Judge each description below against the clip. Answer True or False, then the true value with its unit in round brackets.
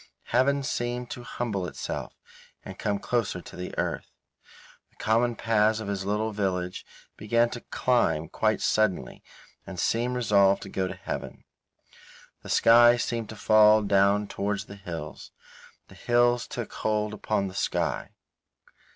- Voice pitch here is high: False (105 Hz)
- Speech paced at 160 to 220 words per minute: False (145 wpm)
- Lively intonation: False (3.4 semitones)